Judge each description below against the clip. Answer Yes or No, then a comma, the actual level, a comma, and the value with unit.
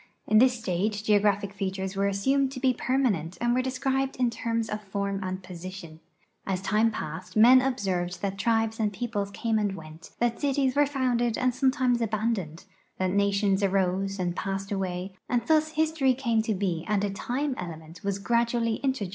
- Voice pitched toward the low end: No, high, 210 Hz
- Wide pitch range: No, average, 4.2 semitones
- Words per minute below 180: No, average, 185 wpm